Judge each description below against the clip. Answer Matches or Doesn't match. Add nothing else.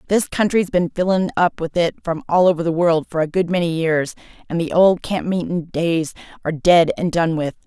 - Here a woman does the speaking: Matches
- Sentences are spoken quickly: Matches